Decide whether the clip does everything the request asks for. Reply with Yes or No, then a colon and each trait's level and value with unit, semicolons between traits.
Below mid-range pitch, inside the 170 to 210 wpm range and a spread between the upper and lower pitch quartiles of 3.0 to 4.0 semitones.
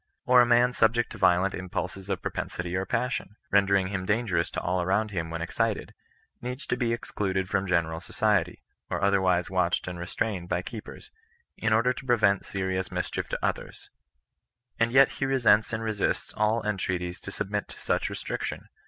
Yes: low, 100 Hz; average, 190 wpm; average, 3.6 semitones